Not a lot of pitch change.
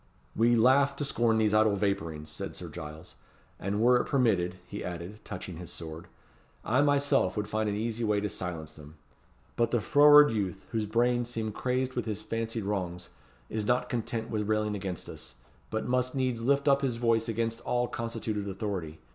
No: average, 3.7 semitones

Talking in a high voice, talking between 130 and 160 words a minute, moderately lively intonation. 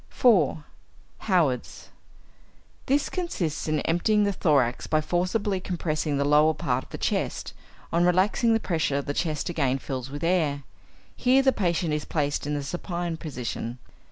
No: medium, 160 Hz; average, 155 wpm; average, 4.2 semitones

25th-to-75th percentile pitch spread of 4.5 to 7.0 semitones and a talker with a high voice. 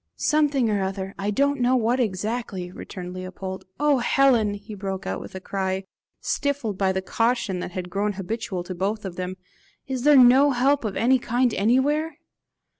Yes: average, 5.3 semitones; high, 210 Hz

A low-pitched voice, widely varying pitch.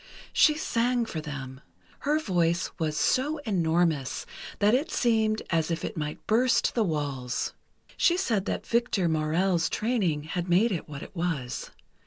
No: medium, 175 Hz; wide, 6.8 semitones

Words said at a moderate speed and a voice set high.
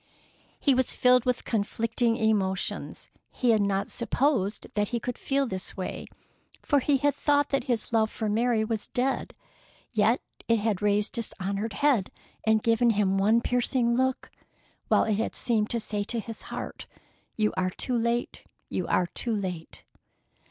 Yes: average, 165 wpm; high, 225 Hz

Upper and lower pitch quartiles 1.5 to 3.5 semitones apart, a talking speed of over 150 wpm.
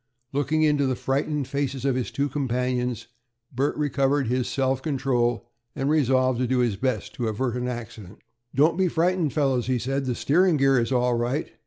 Yes: narrow, 2.5 semitones; average, 185 wpm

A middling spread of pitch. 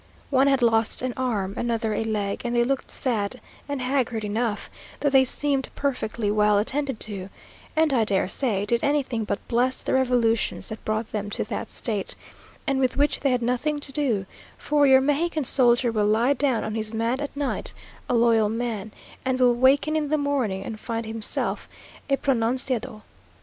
Yes: average, 3.8 semitones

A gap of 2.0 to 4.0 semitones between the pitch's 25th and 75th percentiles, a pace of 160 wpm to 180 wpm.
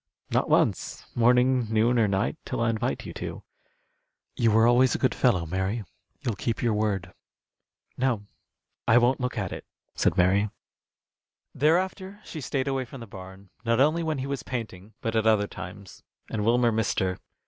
Yes: average, 3.7 semitones; average, 175 wpm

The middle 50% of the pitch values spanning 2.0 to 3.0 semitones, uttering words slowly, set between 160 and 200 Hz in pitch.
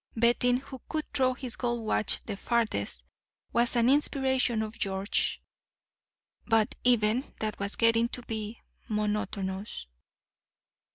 No: average, 2.7 semitones; slow, 120 wpm; high, 230 Hz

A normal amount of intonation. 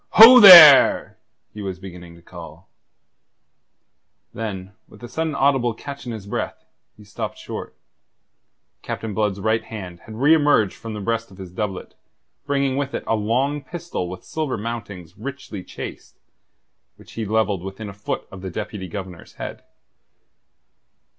No: wide, 6.0 semitones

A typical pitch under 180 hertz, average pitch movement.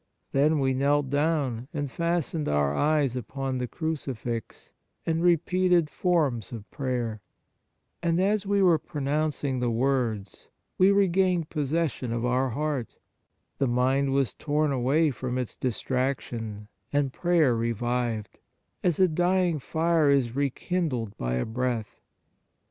Yes: medium, 140 Hz; average, 4.8 semitones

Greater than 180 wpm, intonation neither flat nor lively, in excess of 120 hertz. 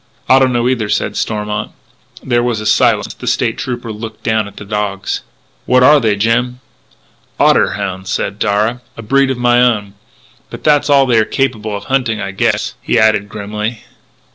No: average, 190 wpm; average, 3.0 semitones; low, 110 Hz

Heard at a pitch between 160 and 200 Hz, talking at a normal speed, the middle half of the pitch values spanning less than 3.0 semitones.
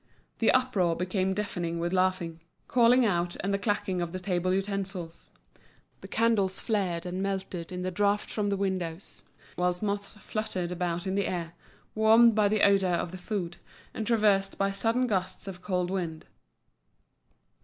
Yes: high, 190 Hz; average, 165 wpm; narrow, 2.6 semitones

